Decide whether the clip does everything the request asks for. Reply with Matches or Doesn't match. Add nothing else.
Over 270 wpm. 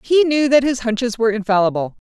Doesn't match